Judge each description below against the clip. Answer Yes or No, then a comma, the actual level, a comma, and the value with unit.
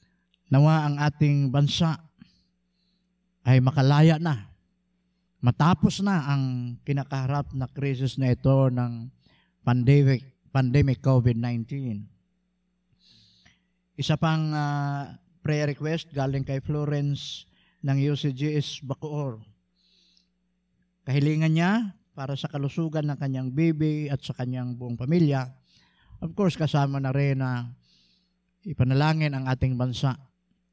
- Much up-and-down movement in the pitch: No, average, 3.7 semitones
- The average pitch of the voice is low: No, medium, 145 Hz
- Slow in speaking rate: Yes, slow, 105 wpm